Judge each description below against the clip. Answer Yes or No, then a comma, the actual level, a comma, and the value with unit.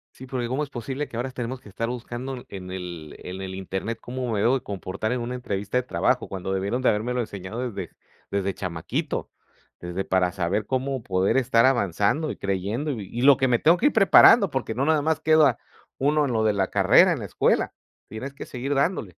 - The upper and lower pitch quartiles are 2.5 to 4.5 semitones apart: No, average, 5.3 semitones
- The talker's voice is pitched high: No, low, 120 Hz